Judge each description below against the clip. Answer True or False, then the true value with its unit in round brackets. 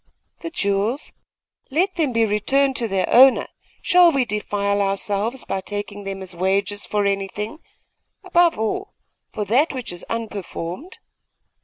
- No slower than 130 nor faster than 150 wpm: True (140 wpm)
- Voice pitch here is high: True (210 Hz)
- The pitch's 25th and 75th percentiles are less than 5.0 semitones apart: False (5.4 semitones)